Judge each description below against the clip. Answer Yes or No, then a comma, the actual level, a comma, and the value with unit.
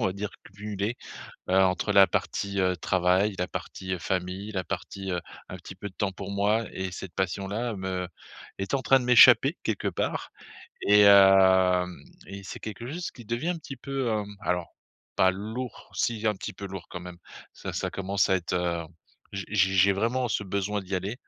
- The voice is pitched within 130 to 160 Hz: No, low, 100 Hz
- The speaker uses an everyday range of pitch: No, narrow, 2.3 semitones